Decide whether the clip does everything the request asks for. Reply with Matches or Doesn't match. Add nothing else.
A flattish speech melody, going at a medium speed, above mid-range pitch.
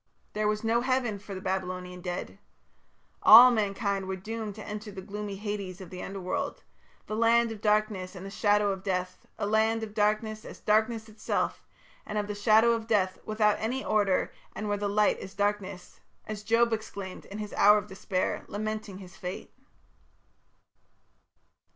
Matches